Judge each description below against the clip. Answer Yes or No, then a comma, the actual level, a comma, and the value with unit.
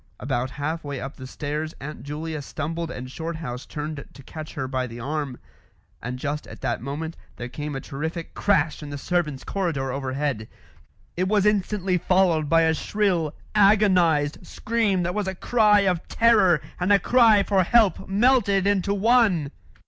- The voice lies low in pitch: No, medium, 165 Hz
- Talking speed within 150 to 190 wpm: Yes, average, 170 wpm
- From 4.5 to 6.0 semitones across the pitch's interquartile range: Yes, wide, 5.4 semitones